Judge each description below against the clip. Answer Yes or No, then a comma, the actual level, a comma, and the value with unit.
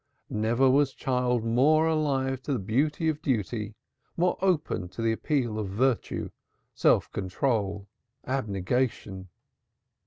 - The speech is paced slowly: Yes, slow, 120 wpm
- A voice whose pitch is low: Yes, low, 125 Hz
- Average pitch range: Yes, average, 4.7 semitones